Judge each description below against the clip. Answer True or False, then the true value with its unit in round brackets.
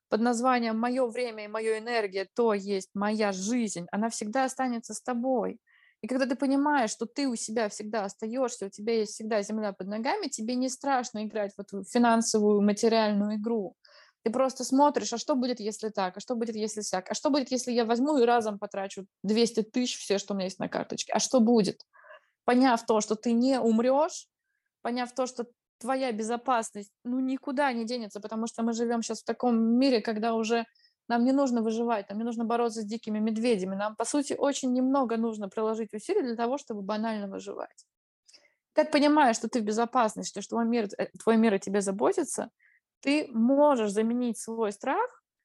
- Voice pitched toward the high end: True (230 Hz)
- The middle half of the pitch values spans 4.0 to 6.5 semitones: False (2.8 semitones)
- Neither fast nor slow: False (190 wpm)